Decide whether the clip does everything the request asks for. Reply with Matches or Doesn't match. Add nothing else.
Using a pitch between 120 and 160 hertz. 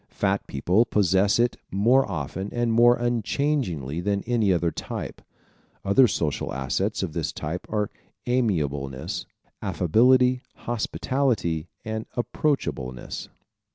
Doesn't match